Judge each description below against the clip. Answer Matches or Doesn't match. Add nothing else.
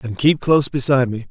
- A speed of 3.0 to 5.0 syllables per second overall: Doesn't match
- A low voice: Matches